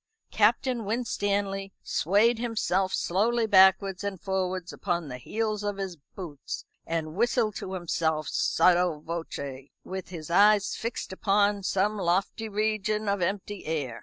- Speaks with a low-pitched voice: No, high, 195 Hz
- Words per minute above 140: No, slow, 135 wpm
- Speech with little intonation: No, average, 3.3 semitones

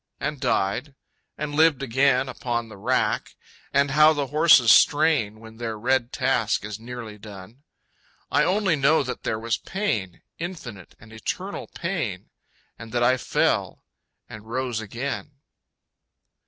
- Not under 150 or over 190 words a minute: No, average, 140 wpm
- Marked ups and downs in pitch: No, average, 4.8 semitones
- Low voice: Yes, low, 125 Hz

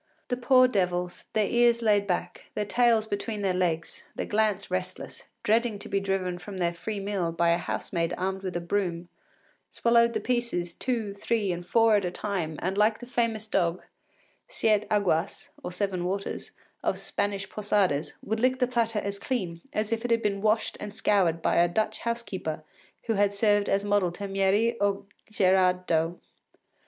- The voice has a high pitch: Yes, high, 200 Hz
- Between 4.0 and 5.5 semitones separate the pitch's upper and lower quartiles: No, average, 3.4 semitones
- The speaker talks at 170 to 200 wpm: Yes, average, 180 wpm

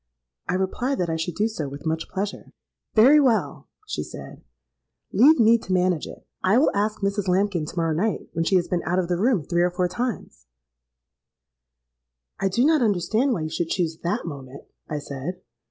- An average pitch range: No, wide, 6.3 semitones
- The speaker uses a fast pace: No, average, 185 wpm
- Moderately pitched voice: Yes, medium, 180 Hz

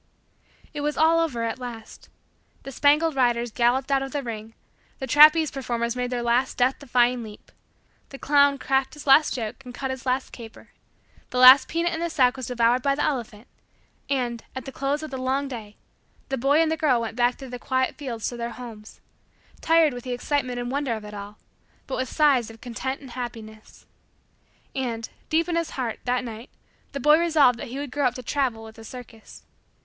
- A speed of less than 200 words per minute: No, fast, 205 wpm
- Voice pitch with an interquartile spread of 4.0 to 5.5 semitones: No, average, 3.0 semitones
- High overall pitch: Yes, very high, 255 Hz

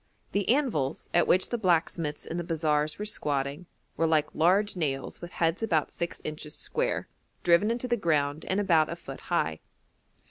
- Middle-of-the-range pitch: Yes, medium, 165 Hz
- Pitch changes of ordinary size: Yes, average, 3.8 semitones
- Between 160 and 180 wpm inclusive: Yes, average, 175 wpm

